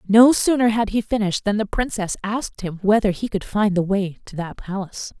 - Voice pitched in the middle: No, high, 205 Hz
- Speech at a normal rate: No, fast, 220 wpm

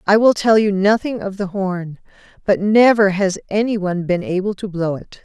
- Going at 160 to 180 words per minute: No, fast, 205 wpm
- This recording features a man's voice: No, female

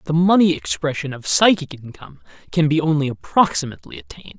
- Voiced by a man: Yes, male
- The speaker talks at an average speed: Yes, average, 150 wpm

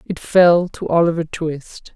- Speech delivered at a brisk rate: No, average, 155 wpm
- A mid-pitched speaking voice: Yes, medium, 165 Hz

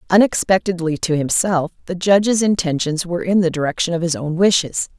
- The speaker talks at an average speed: Yes, average, 170 wpm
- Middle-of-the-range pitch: Yes, medium, 175 Hz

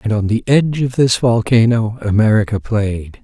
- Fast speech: No, average, 165 wpm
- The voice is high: No, low, 115 Hz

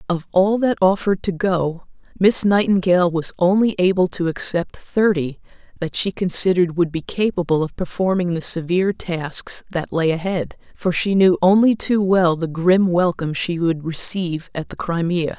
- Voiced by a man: No, female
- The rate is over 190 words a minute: No, average, 170 wpm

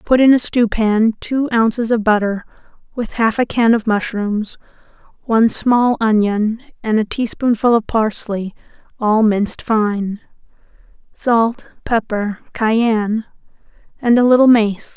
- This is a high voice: Yes, high, 225 Hz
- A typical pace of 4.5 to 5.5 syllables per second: No, 4.1 syllables/s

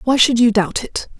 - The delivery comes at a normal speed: No, fast, 250 wpm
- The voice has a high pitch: Yes, high, 235 Hz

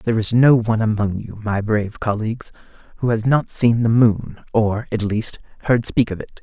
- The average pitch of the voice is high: No, low, 110 Hz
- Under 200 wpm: No, fast, 205 wpm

